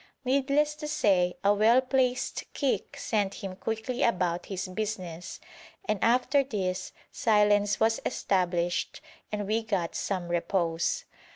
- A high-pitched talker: Yes, high, 205 Hz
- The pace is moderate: No, slow, 125 wpm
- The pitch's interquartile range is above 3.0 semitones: Yes, average, 4.9 semitones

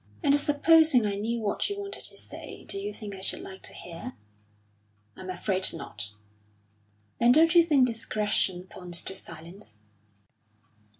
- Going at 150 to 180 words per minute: Yes, average, 155 wpm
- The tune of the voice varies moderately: No, wide, 7.8 semitones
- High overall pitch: Yes, high, 210 Hz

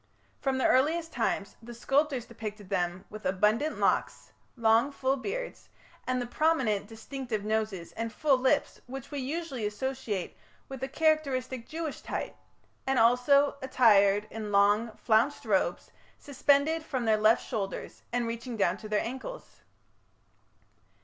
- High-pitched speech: Yes, high, 245 Hz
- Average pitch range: Yes, average, 4.4 semitones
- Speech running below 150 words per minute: Yes, average, 140 wpm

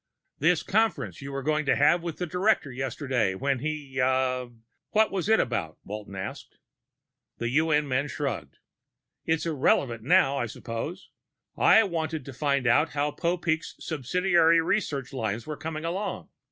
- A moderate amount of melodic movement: Yes, average, 4.4 semitones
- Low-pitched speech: No, medium, 145 Hz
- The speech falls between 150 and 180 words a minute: Yes, average, 155 wpm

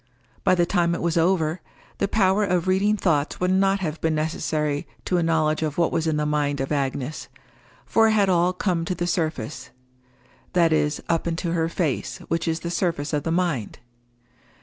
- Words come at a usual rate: Yes, average, 195 wpm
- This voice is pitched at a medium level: Yes, medium, 165 Hz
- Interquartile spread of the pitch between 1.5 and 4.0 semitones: Yes, average, 3.1 semitones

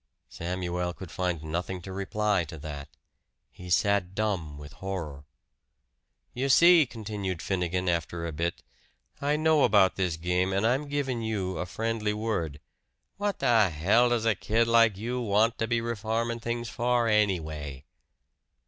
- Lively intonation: No, average, 4.8 semitones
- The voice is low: Yes, low, 100 Hz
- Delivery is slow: No, average, 150 wpm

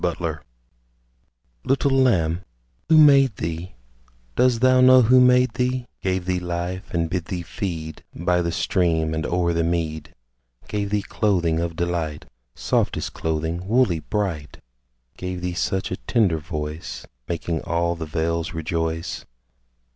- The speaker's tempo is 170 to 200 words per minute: No, average, 140 wpm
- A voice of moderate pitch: No, very low, 85 Hz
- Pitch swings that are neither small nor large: Yes, average, 4.1 semitones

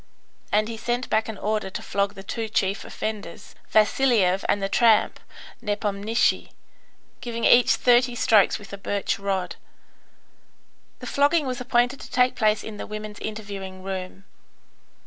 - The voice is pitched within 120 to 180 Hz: No, high, 215 Hz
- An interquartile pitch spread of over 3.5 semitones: No, average, 3.2 semitones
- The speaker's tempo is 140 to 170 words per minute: Yes, average, 145 wpm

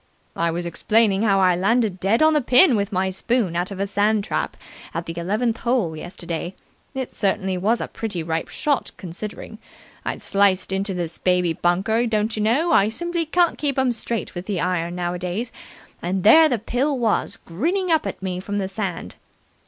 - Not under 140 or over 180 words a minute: No, average, 190 wpm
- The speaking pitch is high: Yes, high, 200 Hz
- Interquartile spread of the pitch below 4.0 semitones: No, average, 4.5 semitones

